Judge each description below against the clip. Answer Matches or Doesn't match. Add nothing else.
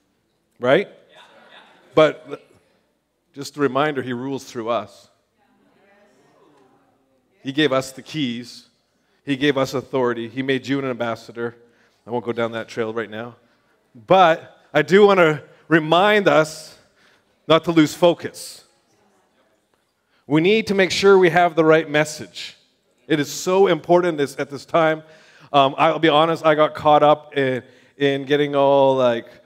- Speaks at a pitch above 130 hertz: Matches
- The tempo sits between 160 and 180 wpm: Doesn't match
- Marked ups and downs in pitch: Doesn't match